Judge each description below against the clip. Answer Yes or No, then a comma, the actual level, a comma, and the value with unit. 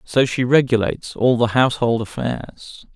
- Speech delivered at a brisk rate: No, average, 140 wpm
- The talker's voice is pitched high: No, low, 120 Hz